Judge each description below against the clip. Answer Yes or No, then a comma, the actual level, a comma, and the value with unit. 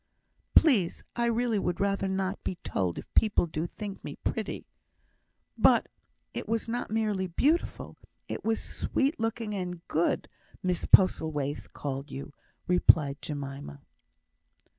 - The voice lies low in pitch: No, high, 190 Hz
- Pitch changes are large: Yes, wide, 6.3 semitones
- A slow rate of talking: Yes, slow, 130 wpm